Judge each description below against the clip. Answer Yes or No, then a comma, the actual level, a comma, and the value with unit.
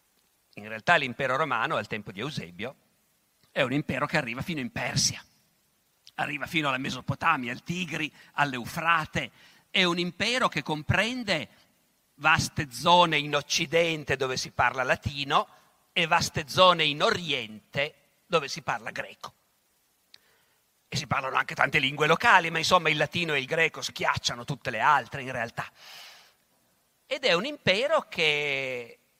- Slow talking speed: No, average, 145 wpm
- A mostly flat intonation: No, average, 4.1 semitones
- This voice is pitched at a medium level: Yes, medium, 155 Hz